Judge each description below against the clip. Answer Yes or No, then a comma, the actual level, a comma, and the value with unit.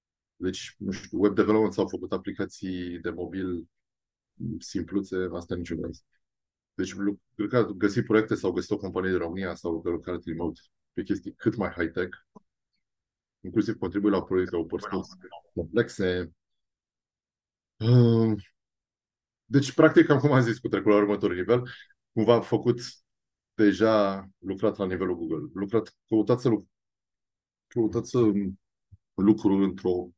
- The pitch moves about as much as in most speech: Yes, average, 3.6 semitones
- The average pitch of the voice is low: Yes, low, 100 Hz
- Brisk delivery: No, average, 130 wpm